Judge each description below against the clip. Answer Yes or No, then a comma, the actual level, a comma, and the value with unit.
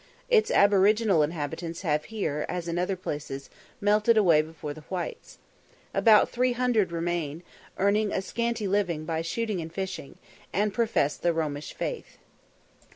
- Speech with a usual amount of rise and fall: Yes, average, 4.8 semitones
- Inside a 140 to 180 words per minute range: Yes, average, 145 wpm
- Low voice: No, medium, 180 Hz